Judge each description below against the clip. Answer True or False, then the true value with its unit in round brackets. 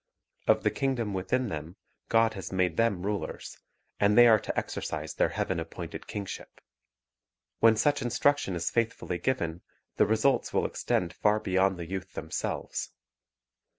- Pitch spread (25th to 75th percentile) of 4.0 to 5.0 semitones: True (4.4 semitones)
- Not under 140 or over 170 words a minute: True (150 wpm)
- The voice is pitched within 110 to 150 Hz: False (100 Hz)